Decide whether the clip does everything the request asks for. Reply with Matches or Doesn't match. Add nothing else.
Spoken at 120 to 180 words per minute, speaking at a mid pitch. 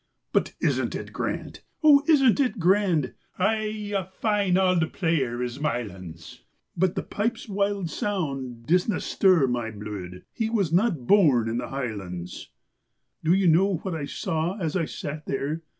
Matches